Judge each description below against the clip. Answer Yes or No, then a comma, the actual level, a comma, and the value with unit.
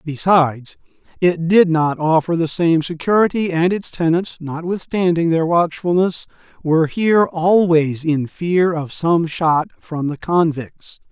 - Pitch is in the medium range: Yes, medium, 165 Hz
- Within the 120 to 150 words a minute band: Yes, slow, 135 wpm